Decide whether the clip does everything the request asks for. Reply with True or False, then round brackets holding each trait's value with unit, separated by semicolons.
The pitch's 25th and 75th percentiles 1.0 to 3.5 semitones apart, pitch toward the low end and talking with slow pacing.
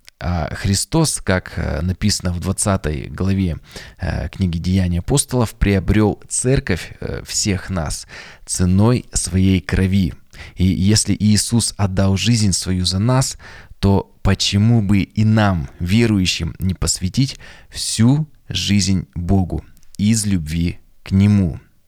True (2.6 semitones; 95 Hz; 105 wpm)